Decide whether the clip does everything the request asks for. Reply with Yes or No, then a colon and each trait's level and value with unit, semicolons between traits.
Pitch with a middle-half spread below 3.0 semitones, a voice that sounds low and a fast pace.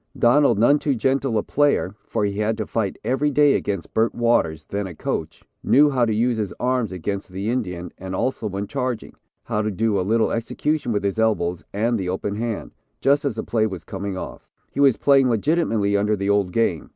No: average, 4.1 semitones; low, 110 Hz; fast, 210 wpm